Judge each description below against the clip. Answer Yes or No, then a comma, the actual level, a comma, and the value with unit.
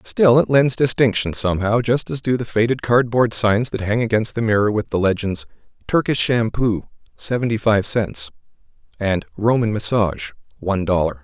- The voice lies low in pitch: Yes, low, 110 Hz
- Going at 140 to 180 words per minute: Yes, average, 160 wpm